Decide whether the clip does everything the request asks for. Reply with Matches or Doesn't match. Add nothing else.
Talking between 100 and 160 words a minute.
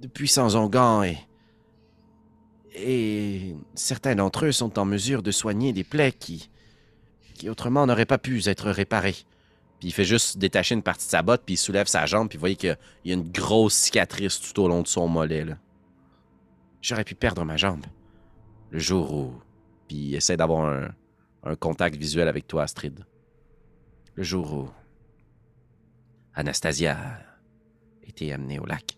Doesn't match